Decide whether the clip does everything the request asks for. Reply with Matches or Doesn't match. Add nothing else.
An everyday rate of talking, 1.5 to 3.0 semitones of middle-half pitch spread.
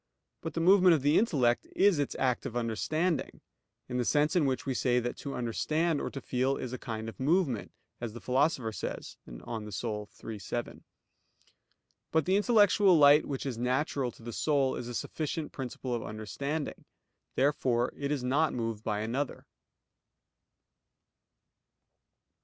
Doesn't match